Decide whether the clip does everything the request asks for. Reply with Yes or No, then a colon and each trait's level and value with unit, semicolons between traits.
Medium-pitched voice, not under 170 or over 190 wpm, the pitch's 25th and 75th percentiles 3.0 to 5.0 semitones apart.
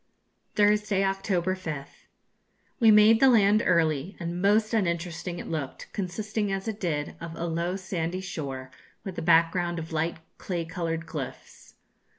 No: medium, 175 Hz; average, 150 wpm; average, 3.5 semitones